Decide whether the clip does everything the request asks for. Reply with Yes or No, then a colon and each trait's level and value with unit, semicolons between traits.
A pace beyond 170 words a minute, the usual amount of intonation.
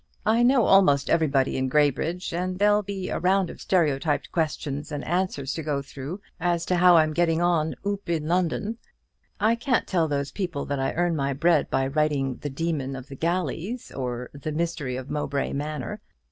Yes: average, 190 wpm; average, 4.3 semitones